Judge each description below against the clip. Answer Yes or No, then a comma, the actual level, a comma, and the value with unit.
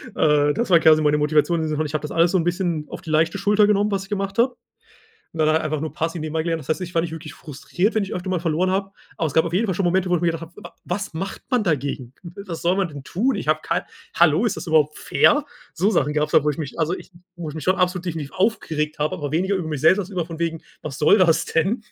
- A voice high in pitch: No, medium, 170 Hz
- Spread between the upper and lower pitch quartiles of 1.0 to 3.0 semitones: No, average, 3.5 semitones